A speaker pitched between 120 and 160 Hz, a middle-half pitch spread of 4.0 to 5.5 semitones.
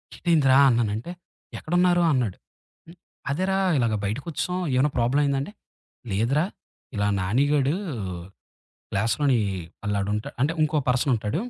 Yes: low, 135 Hz; average, 5.1 semitones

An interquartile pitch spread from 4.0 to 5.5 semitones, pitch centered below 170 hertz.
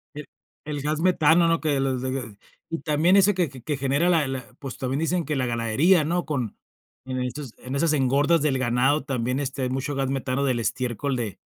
No: average, 3.2 semitones; medium, 140 Hz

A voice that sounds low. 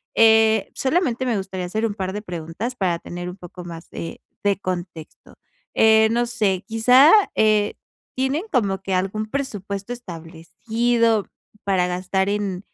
No: high, 205 Hz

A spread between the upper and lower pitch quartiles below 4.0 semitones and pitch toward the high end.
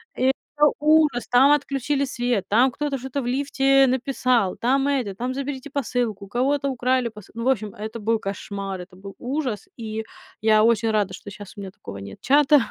No: average, 4.4 semitones; high, 245 Hz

